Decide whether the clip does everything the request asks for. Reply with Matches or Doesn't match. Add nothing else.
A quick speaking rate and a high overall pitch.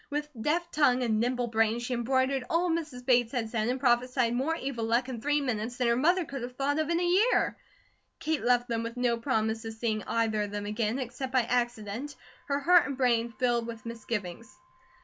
Matches